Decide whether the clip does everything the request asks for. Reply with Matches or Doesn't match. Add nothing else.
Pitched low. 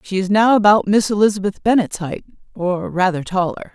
Doesn't match